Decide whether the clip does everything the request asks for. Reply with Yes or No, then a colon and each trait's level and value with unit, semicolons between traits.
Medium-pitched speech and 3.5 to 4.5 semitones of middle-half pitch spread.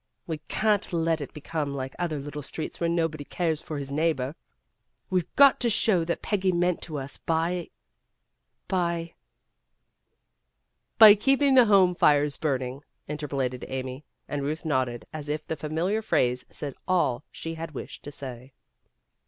Yes: medium, 155 Hz; average, 3.8 semitones